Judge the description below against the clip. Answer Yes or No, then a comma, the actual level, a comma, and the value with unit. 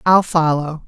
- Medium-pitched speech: Yes, medium, 165 Hz